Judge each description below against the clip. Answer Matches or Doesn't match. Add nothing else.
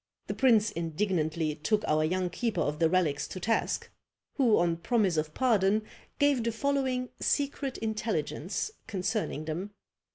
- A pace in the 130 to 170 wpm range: Matches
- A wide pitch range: Matches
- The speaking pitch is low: Doesn't match